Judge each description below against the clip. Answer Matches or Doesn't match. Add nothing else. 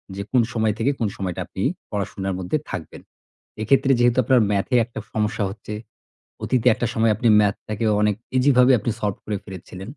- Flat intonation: Doesn't match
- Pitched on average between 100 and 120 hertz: Matches